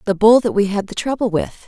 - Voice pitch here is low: No, high, 210 Hz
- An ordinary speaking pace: No, fast, 285 wpm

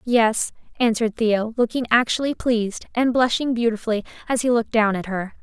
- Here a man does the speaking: No, female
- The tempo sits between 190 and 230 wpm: No, average, 165 wpm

